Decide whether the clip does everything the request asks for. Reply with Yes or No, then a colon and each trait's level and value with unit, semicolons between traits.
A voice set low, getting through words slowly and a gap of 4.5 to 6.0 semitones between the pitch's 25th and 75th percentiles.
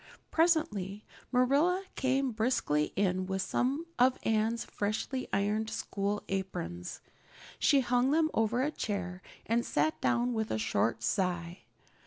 No: high, 220 Hz; slow, 130 wpm; average, 5.2 semitones